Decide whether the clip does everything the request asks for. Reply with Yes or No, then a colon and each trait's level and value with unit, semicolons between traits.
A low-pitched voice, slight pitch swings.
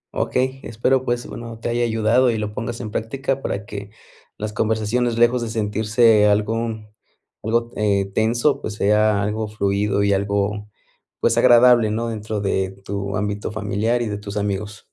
Yes: low, 110 Hz; narrow, 2.2 semitones